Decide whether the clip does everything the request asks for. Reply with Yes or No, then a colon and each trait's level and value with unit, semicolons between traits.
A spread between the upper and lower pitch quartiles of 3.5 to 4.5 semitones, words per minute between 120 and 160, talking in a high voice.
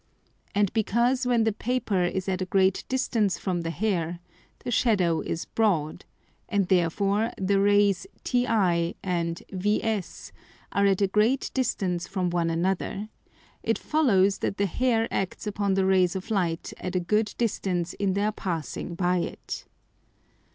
No: average, 3.1 semitones; average, 150 wpm; high, 195 Hz